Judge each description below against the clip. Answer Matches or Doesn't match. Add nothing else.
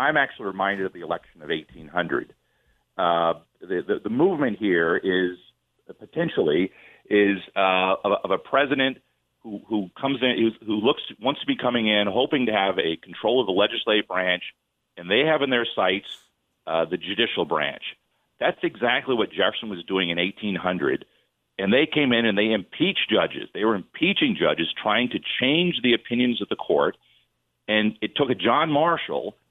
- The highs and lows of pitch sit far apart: Doesn't match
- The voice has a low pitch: Matches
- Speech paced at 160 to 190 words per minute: Matches